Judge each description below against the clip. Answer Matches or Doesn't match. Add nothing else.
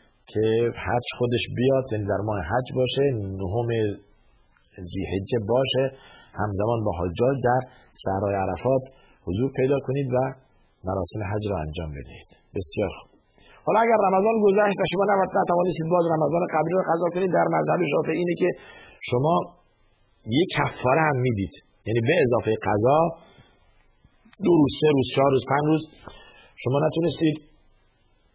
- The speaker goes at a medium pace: Matches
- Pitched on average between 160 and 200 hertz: Doesn't match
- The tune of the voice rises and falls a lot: Matches